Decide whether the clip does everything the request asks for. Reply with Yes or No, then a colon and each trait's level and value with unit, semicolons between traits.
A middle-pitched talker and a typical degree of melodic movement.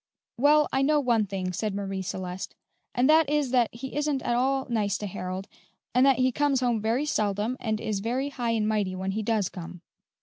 No: high, 230 Hz; average, 5.0 semitones